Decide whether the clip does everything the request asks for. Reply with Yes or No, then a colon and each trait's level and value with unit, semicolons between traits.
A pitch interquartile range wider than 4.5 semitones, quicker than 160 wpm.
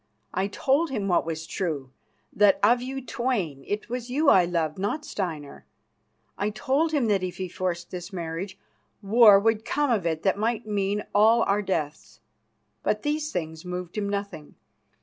Yes: average, 4.9 semitones; average, 170 wpm